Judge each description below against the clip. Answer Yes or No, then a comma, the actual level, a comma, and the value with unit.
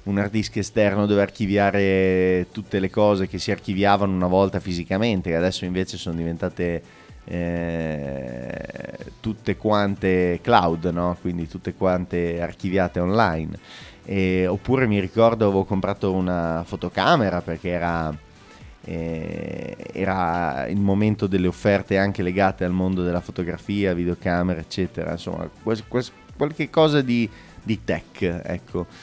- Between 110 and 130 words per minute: Yes, average, 125 wpm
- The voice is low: Yes, very low, 95 Hz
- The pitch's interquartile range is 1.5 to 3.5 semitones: Yes, narrow, 2.5 semitones